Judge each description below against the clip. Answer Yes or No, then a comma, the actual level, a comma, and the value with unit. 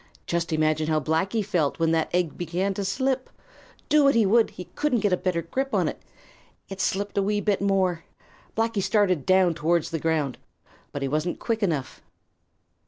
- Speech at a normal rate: Yes, average, 185 wpm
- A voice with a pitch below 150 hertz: No, medium, 185 Hz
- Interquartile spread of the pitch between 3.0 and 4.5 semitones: Yes, average, 4.2 semitones